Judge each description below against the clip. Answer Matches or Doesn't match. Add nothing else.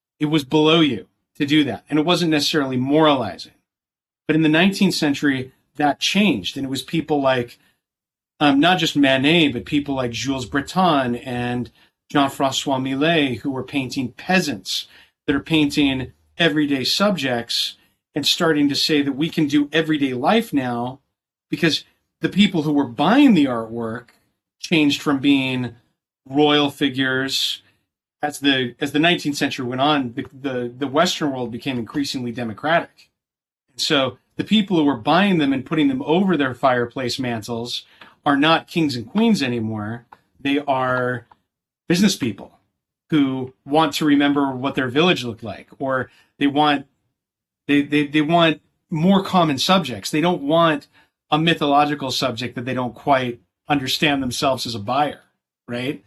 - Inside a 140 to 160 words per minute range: Matches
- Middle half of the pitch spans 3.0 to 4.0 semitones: Matches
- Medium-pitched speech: Matches